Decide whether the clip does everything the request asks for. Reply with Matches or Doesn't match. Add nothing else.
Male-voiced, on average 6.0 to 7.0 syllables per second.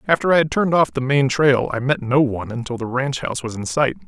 Matches